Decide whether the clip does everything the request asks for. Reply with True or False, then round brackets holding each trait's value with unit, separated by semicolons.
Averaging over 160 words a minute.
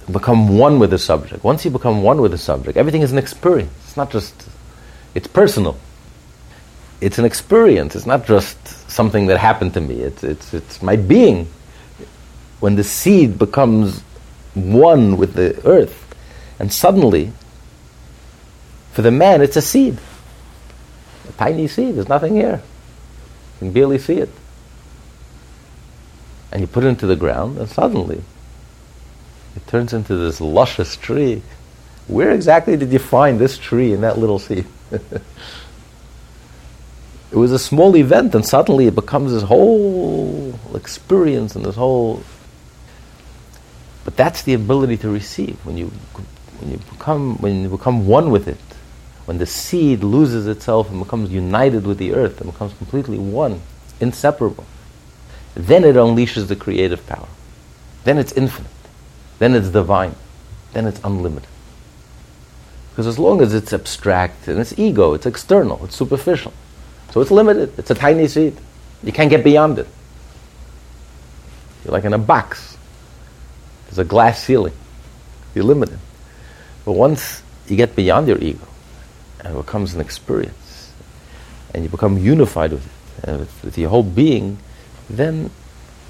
False (150 wpm)